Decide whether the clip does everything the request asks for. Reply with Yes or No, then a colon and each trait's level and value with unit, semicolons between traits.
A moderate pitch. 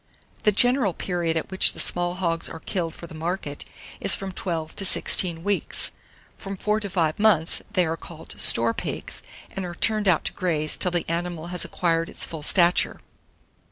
Yes: medium, 175 Hz